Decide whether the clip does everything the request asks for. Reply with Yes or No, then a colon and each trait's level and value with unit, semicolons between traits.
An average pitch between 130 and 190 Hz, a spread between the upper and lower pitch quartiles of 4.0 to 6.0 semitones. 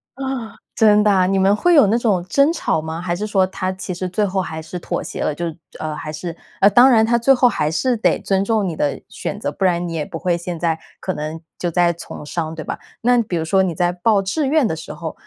Yes: medium, 185 Hz; average, 4.7 semitones